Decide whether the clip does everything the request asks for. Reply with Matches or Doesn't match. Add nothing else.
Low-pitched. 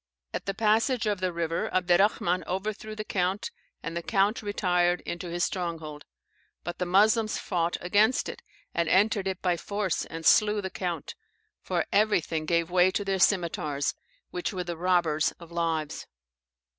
Doesn't match